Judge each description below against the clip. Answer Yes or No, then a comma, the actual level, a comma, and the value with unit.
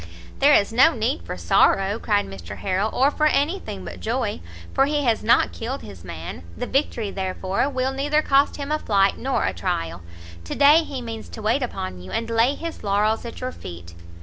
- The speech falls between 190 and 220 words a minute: Yes, fast, 205 wpm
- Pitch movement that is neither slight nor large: No, wide, 6.7 semitones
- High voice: Yes, high, 225 Hz